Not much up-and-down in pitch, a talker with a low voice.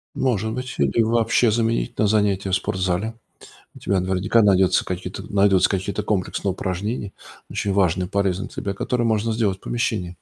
No: average, 3.0 semitones; low, 100 Hz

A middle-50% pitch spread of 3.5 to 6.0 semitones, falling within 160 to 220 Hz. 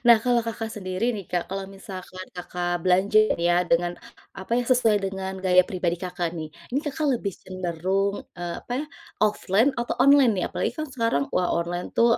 Yes: average, 4.3 semitones; high, 190 Hz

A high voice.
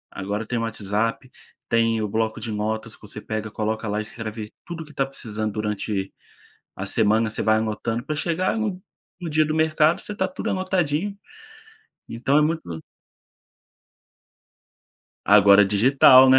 No: low, 115 Hz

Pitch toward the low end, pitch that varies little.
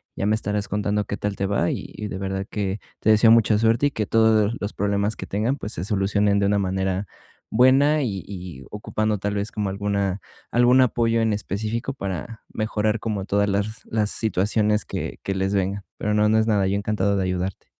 Yes: low, 105 Hz; narrow, 1.8 semitones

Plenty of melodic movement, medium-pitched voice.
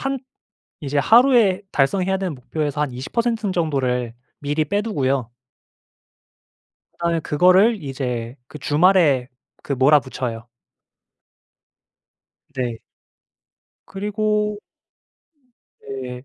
Yes: wide, 6.8 semitones; medium, 150 Hz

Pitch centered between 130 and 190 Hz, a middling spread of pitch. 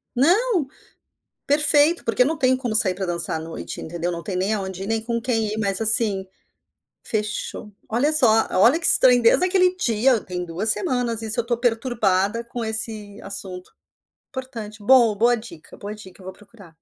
No: high, 225 Hz; average, 4.2 semitones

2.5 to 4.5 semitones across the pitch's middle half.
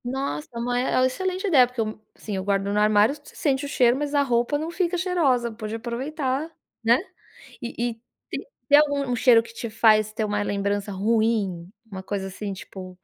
No: average, 4.9 semitones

